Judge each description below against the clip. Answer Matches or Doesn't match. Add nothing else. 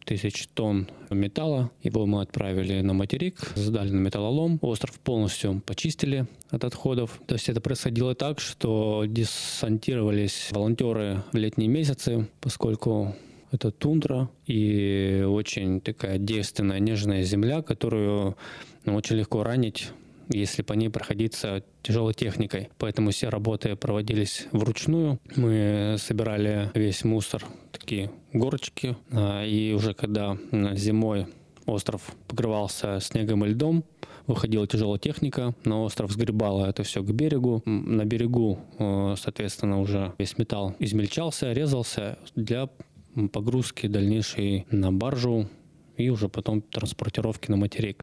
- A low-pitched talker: Matches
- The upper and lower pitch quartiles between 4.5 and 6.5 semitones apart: Doesn't match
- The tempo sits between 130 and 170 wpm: Doesn't match